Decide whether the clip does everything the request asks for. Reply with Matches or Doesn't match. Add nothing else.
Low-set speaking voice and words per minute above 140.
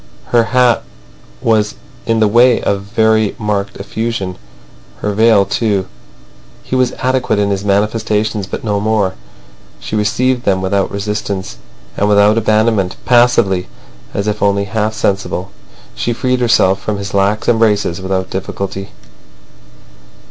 Doesn't match